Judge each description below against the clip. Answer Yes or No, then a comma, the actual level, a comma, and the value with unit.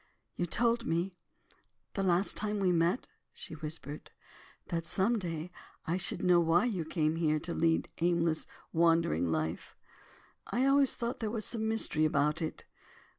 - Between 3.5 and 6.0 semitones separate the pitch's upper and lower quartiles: Yes, average, 4.5 semitones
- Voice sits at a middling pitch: Yes, medium, 170 Hz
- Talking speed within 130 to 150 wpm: No, average, 160 wpm